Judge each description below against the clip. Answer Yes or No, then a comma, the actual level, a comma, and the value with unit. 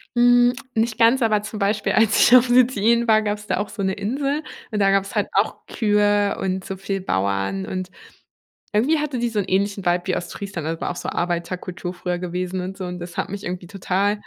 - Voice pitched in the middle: No, high, 200 Hz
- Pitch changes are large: No, average, 3.3 semitones